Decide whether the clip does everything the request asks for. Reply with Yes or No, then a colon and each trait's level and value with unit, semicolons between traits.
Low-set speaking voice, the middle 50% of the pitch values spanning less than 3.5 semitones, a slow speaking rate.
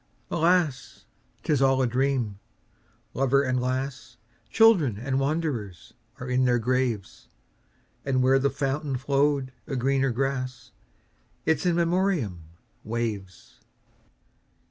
Yes: low, 130 Hz; average, 2.7 semitones; slow, 100 wpm